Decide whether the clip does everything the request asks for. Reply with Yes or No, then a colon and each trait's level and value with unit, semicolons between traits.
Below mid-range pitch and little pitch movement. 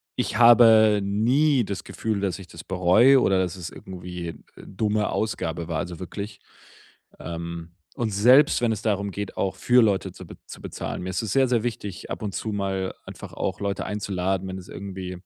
No: low, 100 Hz; average, 3.0 semitones